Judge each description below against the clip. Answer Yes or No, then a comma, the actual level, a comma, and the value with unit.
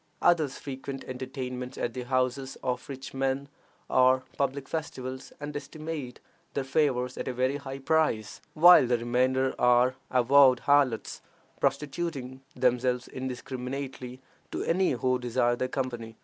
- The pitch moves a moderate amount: No, narrow, 1.8 semitones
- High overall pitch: No, low, 130 Hz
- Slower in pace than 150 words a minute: Yes, slow, 135 wpm